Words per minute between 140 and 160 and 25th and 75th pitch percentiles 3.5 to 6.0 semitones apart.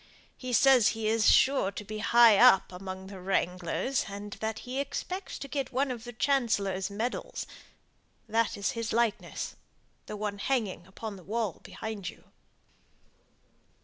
Yes: average, 150 wpm; average, 3.8 semitones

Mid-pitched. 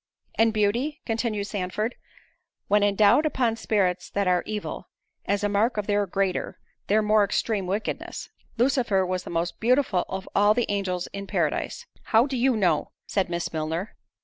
No: high, 205 Hz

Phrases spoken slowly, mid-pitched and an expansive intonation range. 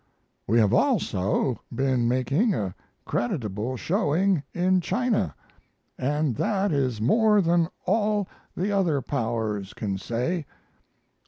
Yes: slow, 110 wpm; medium, 145 Hz; wide, 8.5 semitones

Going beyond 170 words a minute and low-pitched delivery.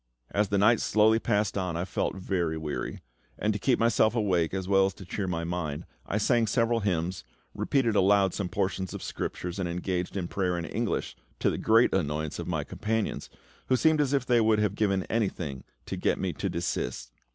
Yes: fast, 205 wpm; very low, 95 Hz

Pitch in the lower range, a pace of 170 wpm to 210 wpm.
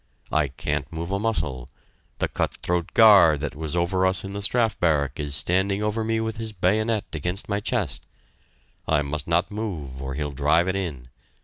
Yes: very low, 90 Hz; average, 190 wpm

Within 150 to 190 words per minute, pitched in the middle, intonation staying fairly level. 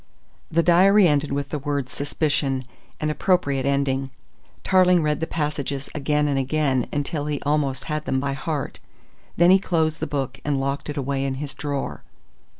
Yes: average, 170 wpm; medium, 145 Hz; narrow, 2.1 semitones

